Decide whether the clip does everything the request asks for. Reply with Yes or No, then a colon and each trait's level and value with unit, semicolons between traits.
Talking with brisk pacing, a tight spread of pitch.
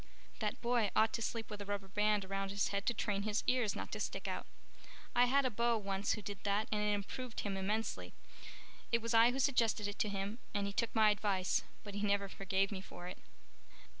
Yes: fast, 225 wpm; narrow, 2.2 semitones